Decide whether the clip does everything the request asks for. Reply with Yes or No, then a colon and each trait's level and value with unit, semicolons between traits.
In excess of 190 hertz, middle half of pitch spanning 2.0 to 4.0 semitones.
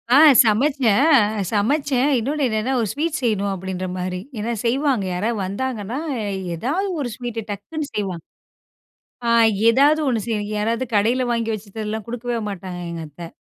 No: high, 225 Hz; average, 4.5 semitones